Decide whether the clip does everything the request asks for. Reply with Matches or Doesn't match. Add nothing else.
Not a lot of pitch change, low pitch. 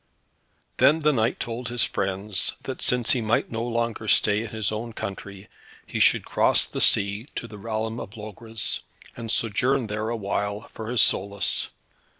Matches